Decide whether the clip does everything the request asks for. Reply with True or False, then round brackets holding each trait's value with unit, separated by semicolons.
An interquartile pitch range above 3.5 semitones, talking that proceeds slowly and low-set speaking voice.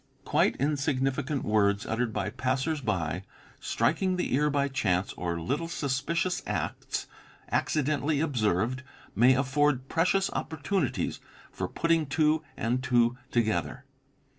True (4.6 semitones; 120 wpm; 130 Hz)